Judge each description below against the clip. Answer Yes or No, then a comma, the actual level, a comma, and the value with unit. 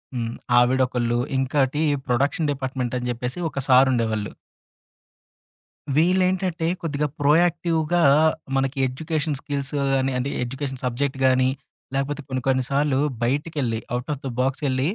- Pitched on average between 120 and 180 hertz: Yes, low, 135 Hz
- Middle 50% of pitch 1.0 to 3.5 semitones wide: Yes, average, 2.7 semitones